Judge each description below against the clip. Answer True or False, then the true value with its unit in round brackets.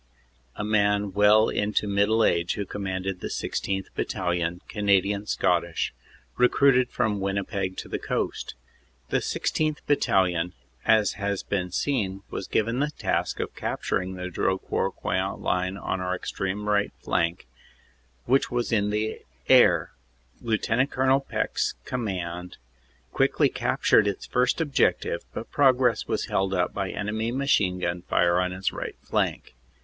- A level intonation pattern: False (3.2 semitones)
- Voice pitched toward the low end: True (100 Hz)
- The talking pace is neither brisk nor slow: True (145 wpm)